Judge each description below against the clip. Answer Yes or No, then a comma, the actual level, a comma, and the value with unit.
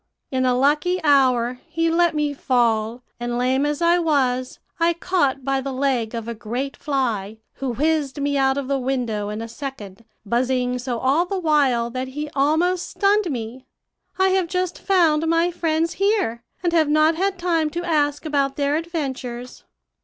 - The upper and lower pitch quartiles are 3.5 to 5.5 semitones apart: Yes, average, 4.8 semitones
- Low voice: No, very high, 280 Hz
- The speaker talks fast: No, average, 175 wpm